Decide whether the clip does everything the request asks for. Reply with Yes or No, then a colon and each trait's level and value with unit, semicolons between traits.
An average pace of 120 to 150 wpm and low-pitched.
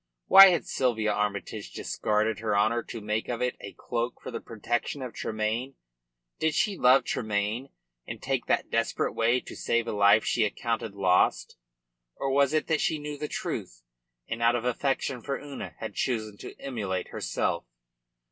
No: average, 175 wpm; low, 115 Hz